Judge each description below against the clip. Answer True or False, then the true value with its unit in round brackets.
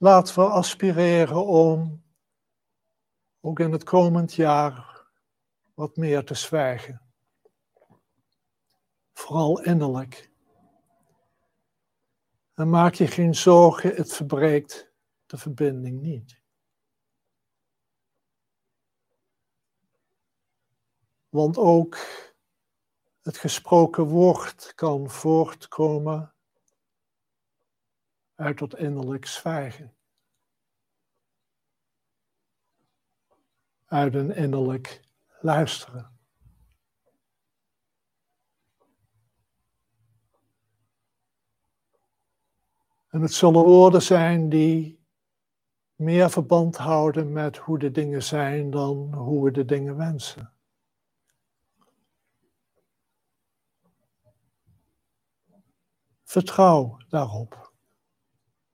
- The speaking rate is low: True (65 wpm)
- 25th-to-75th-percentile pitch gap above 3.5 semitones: True (4.2 semitones)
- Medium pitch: True (150 Hz)